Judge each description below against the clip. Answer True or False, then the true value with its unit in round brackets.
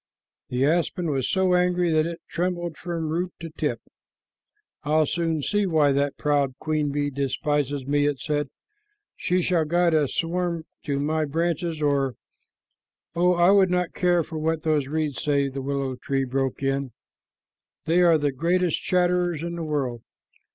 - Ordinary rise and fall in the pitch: True (3.4 semitones)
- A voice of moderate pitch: True (155 Hz)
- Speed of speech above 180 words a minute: False (165 wpm)